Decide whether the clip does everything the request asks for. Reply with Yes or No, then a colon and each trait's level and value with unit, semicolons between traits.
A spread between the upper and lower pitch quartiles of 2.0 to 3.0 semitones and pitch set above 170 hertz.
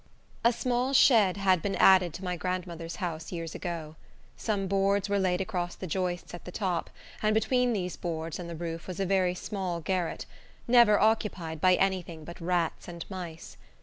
Yes: narrow, 2.6 semitones; medium, 185 Hz